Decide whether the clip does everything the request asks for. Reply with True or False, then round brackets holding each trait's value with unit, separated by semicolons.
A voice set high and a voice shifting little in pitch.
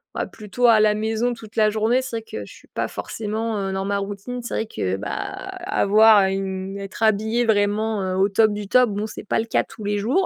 True (215 Hz; 2.1 semitones)